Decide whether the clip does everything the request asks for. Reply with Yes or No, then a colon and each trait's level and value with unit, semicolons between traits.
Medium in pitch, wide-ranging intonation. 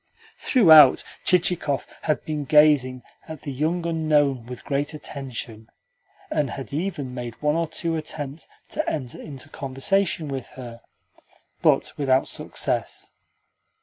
No: medium, 145 Hz; average, 3.3 semitones